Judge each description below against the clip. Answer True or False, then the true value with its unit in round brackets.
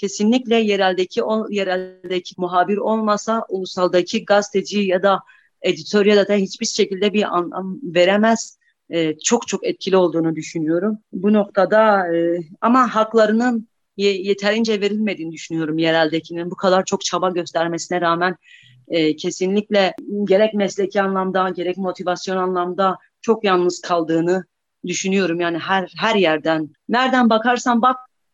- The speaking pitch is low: False (190 Hz)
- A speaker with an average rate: True (125 wpm)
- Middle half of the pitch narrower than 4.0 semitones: True (2.9 semitones)